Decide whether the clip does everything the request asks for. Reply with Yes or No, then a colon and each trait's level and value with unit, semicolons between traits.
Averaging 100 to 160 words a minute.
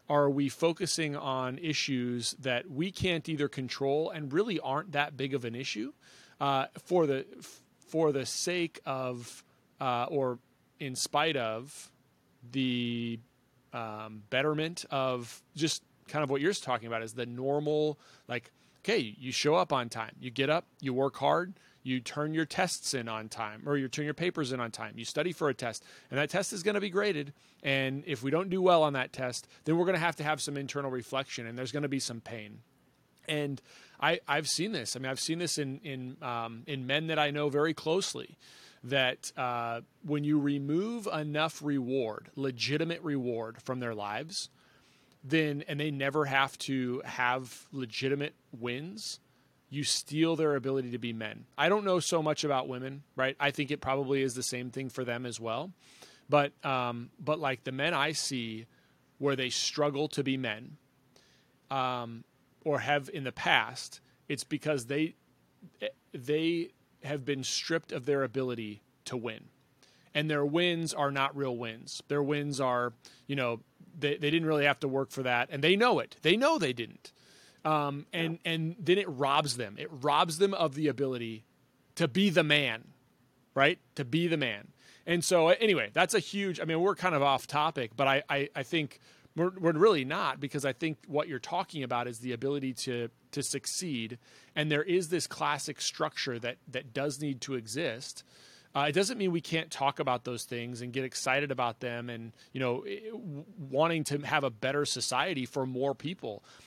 No: average, 190 wpm